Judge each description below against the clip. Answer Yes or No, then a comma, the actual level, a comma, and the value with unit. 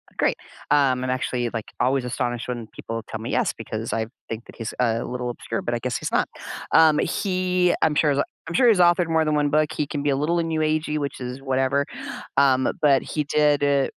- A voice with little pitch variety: No, average, 3.6 semitones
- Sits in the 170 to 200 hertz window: No, medium, 140 Hz